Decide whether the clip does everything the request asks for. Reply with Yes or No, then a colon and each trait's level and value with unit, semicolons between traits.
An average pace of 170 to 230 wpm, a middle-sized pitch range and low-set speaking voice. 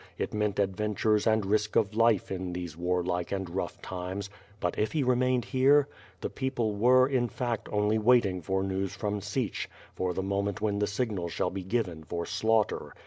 Yes: average, 190 wpm; average, 3.5 semitones; low, 105 Hz